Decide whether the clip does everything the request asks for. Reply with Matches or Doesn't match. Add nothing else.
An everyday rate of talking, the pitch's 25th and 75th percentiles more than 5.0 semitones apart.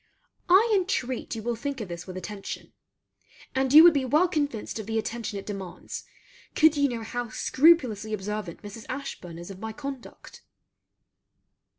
Matches